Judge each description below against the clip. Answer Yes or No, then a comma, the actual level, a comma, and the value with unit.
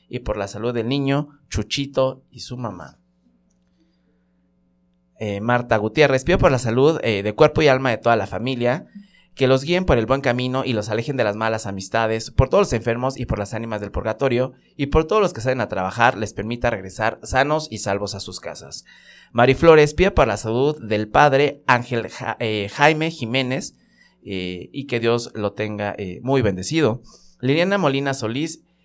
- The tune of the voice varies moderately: Yes, average, 4.5 semitones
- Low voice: Yes, low, 120 Hz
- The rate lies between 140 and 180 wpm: No, fast, 190 wpm